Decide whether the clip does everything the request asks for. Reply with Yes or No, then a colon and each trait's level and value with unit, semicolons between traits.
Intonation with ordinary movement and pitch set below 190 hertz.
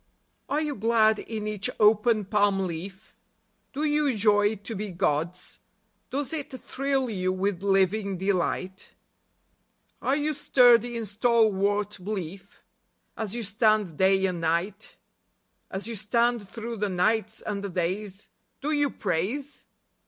No: average, 3.4 semitones; high, 210 Hz